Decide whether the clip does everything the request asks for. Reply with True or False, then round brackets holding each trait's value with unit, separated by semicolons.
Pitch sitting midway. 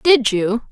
False (240 Hz)